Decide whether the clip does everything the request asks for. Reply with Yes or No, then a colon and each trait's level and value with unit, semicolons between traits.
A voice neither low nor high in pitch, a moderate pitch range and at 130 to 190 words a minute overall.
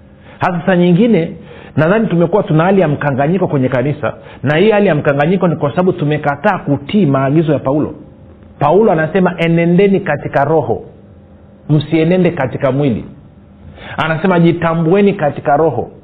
Yes: medium, 155 Hz; average, 4.8 semitones; average, 135 wpm